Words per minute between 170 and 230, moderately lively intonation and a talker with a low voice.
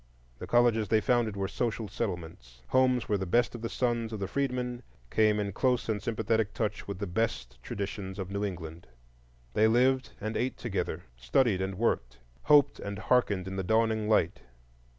Yes: average, 180 wpm; average, 3.7 semitones; low, 110 Hz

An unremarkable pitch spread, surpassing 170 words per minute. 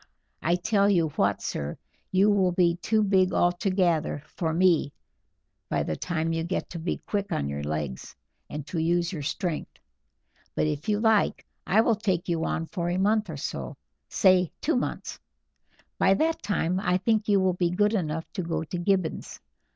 Yes: average, 3.5 semitones; average, 180 wpm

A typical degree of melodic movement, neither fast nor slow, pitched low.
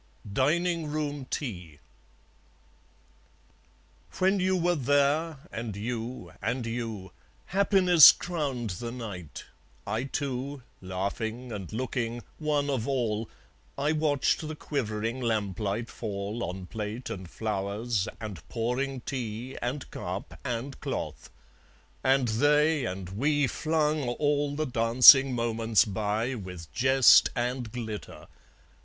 No: average, 4.9 semitones; slow, 110 wpm; low, 120 Hz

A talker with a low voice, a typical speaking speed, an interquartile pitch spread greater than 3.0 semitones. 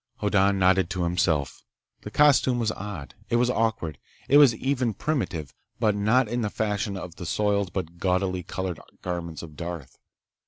Yes: very low, 95 Hz; average, 165 wpm; average, 4.5 semitones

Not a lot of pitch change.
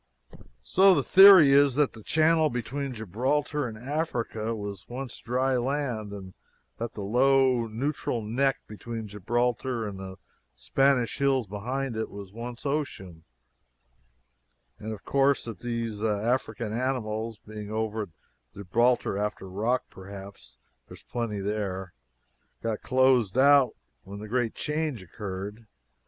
No: average, 4.2 semitones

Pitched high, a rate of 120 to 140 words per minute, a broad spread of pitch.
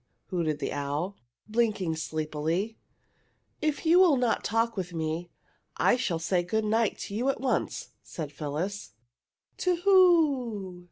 Yes: high, 200 Hz; slow, 135 wpm; wide, 7.2 semitones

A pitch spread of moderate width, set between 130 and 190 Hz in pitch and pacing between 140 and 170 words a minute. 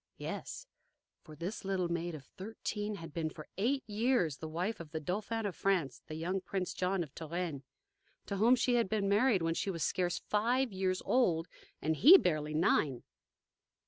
No: average, 4.6 semitones; medium, 185 Hz; average, 180 wpm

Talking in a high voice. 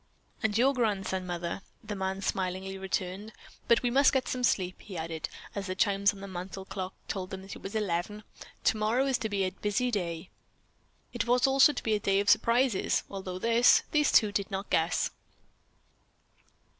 Yes: high, 200 Hz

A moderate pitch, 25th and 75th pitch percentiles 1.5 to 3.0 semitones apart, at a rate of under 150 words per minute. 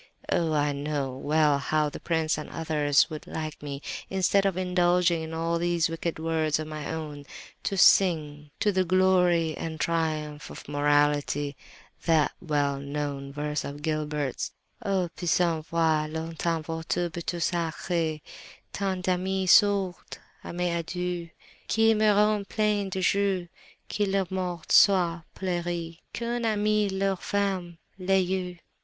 No: medium, 170 Hz; average, 3.5 semitones; average, 140 wpm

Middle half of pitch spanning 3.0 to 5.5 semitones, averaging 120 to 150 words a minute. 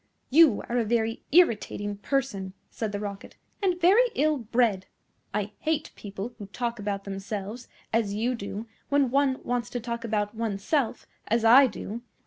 No: average, 4.1 semitones; average, 160 wpm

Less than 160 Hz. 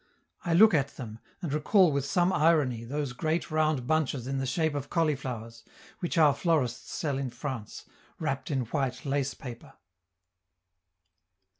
Yes: medium, 140 Hz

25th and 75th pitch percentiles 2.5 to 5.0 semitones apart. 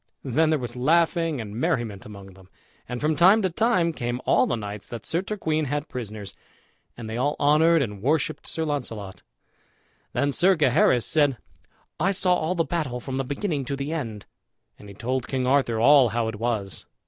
No: wide, 5.6 semitones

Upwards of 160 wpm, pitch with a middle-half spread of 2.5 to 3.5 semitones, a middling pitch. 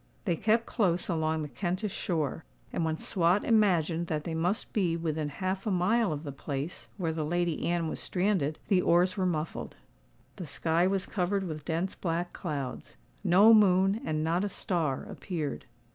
Yes: average, 175 wpm; average, 3.1 semitones; medium, 175 Hz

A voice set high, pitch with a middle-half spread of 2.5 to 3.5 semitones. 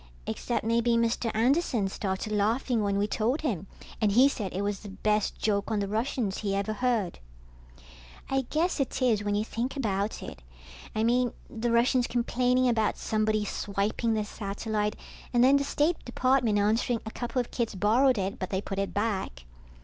Yes: high, 220 Hz; average, 3.2 semitones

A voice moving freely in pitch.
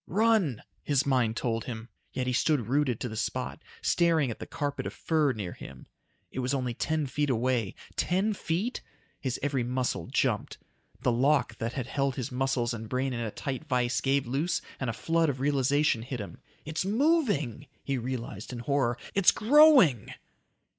No: average, 4.0 semitones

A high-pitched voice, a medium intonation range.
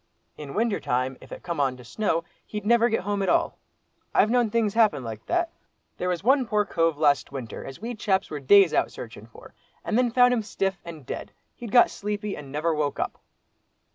No: high, 195 Hz; wide, 7.5 semitones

